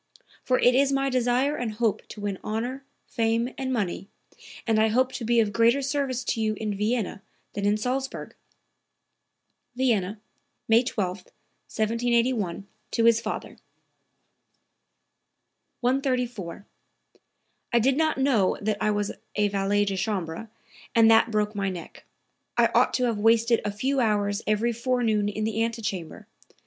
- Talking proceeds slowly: No, average, 145 wpm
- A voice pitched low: No, high, 225 Hz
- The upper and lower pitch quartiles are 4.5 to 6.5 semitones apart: No, average, 3.2 semitones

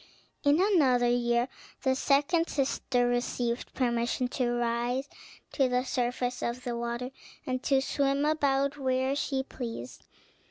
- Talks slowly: Yes, slow, 130 wpm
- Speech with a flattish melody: Yes, narrow, 2.3 semitones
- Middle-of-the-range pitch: No, very high, 255 Hz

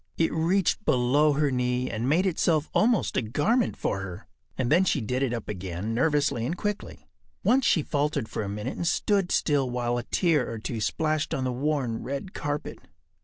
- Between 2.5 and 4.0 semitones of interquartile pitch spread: No, average, 5.1 semitones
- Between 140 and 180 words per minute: No, average, 195 wpm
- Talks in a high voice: No, medium, 140 Hz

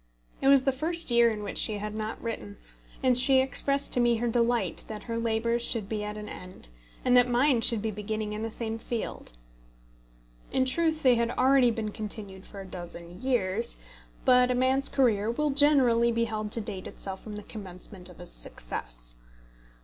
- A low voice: No, high, 230 Hz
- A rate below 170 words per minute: No, average, 195 wpm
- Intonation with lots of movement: No, average, 3.2 semitones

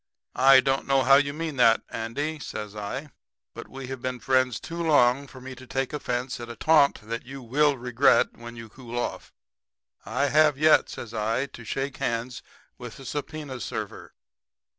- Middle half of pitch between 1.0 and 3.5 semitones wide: Yes, average, 2.9 semitones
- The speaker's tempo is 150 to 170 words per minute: No, average, 185 wpm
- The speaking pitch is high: No, low, 130 Hz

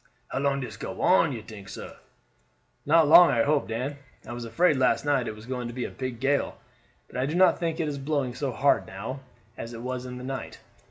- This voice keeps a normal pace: No, fast, 235 wpm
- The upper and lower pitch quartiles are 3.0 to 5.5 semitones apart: Yes, average, 3.3 semitones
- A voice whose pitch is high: No, low, 130 Hz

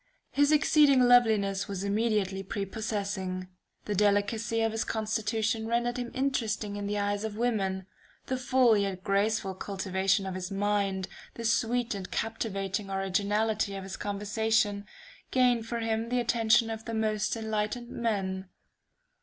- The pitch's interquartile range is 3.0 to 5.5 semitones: No, narrow, 2.5 semitones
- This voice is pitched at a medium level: No, high, 215 Hz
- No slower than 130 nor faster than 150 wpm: Yes, average, 140 wpm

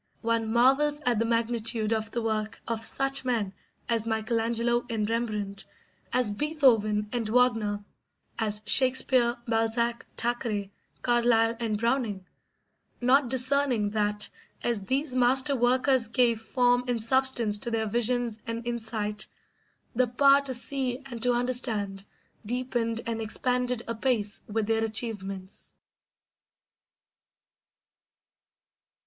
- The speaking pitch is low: No, high, 235 Hz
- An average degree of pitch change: No, narrow, 2.3 semitones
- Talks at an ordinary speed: No, slow, 115 wpm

